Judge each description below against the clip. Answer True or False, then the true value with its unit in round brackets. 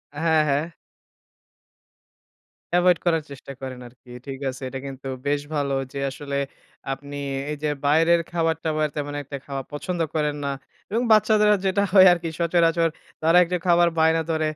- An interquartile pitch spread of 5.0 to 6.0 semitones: False (3.2 semitones)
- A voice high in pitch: False (155 Hz)